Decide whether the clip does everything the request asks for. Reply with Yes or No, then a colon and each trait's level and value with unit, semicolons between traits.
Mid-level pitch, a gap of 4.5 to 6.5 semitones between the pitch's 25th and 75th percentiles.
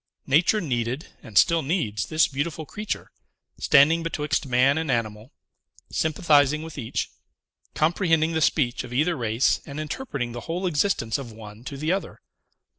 Yes: medium, 145 Hz; average, 4.9 semitones